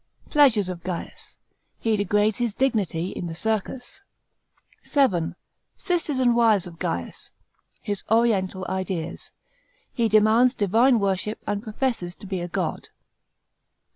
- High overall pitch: Yes, high, 210 Hz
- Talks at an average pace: No, slow, 130 wpm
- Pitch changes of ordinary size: Yes, average, 4.4 semitones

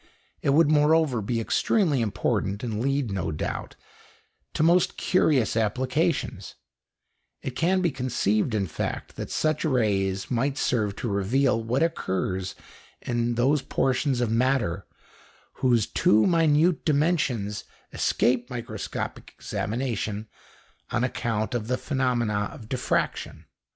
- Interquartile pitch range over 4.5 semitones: Yes, average, 5.0 semitones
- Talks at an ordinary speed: No, slow, 120 wpm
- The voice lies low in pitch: Yes, low, 125 Hz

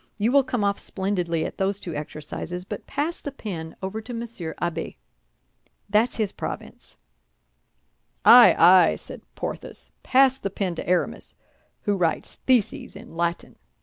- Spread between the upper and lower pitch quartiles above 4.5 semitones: Yes, average, 5.2 semitones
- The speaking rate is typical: Yes, average, 150 wpm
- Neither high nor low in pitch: No, high, 195 Hz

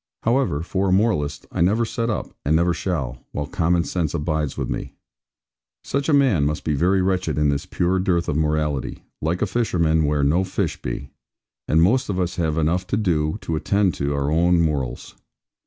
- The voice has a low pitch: Yes, very low, 85 Hz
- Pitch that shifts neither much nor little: Yes, average, 3.8 semitones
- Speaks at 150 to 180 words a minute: No, average, 195 wpm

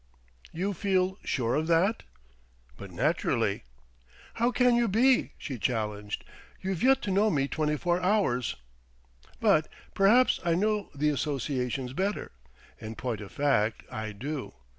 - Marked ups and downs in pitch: Yes, wide, 8.2 semitones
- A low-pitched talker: No, medium, 160 Hz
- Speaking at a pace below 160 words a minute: Yes, average, 140 wpm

